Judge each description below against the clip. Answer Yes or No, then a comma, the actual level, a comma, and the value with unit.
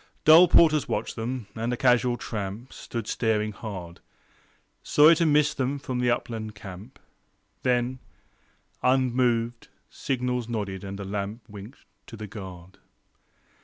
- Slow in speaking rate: Yes, slow, 130 wpm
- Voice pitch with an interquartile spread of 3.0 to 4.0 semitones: Yes, average, 3.6 semitones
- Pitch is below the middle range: Yes, low, 120 Hz